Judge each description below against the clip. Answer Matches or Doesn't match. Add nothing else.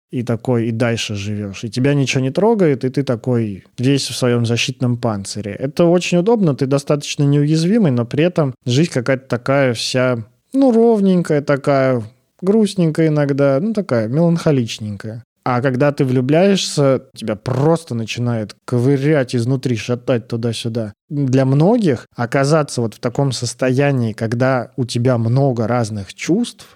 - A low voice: Matches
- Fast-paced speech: Doesn't match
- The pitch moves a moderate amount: Matches